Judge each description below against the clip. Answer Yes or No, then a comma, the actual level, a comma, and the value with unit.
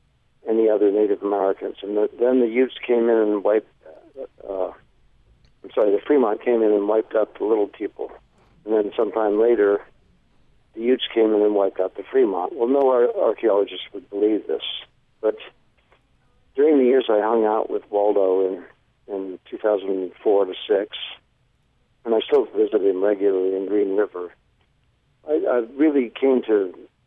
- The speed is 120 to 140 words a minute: No, average, 165 wpm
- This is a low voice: Yes, low, 115 Hz